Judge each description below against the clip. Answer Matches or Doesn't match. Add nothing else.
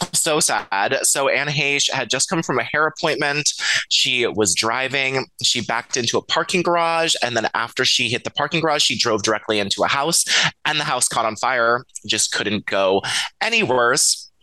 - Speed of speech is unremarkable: Matches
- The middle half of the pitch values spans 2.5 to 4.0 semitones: Doesn't match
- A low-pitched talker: Matches